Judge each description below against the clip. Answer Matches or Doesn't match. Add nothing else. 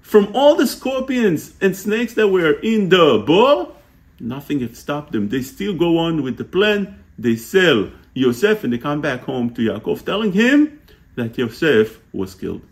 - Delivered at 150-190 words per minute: Matches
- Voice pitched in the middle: Matches